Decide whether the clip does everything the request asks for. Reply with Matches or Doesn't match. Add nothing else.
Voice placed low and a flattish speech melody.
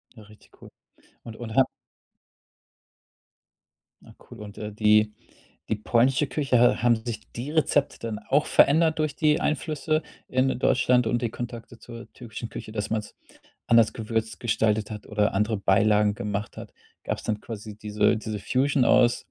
Doesn't match